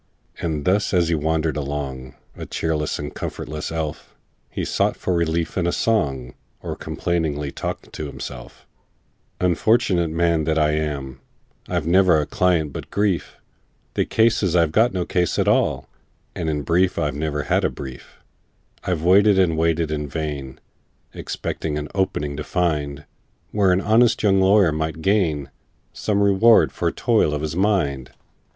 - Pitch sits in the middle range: No, very low, 80 Hz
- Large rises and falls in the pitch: No, average, 3.7 semitones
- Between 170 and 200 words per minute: No, average, 160 wpm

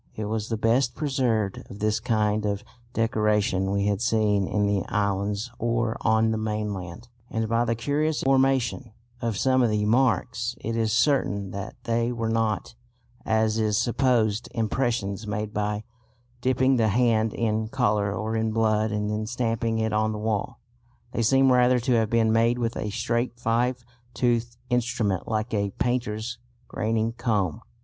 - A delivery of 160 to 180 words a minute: Yes, average, 165 wpm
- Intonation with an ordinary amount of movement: No, narrow, 2.0 semitones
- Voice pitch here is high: No, low, 110 Hz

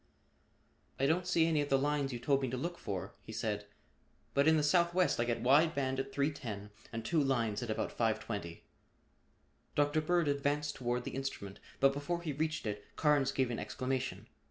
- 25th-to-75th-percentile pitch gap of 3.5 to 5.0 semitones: Yes, average, 4.0 semitones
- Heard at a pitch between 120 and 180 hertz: Yes, low, 135 Hz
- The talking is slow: No, average, 190 wpm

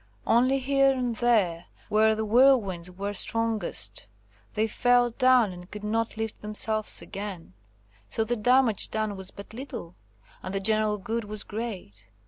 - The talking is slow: No, average, 150 wpm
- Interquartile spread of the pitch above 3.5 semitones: No, average, 3.2 semitones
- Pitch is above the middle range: Yes, high, 215 Hz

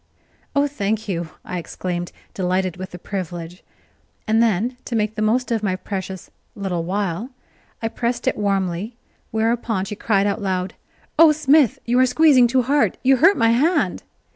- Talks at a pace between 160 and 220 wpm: Yes, average, 165 wpm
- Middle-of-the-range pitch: No, high, 215 Hz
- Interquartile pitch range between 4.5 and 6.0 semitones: Yes, average, 4.8 semitones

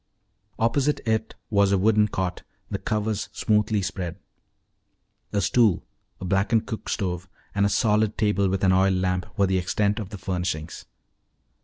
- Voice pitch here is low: Yes, low, 100 Hz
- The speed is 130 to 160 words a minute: Yes, average, 155 wpm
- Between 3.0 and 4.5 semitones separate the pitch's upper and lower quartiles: No, narrow, 2.5 semitones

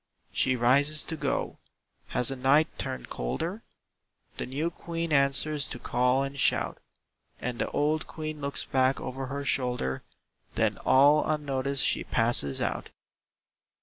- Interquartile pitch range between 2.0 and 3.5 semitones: Yes, average, 3.1 semitones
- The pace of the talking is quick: No, average, 140 wpm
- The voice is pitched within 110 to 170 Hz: Yes, medium, 140 Hz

